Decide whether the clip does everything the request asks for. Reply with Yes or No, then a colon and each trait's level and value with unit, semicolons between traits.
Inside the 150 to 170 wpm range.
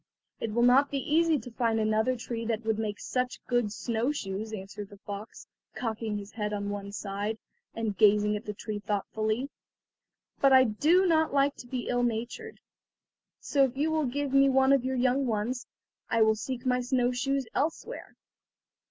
No: average, 185 wpm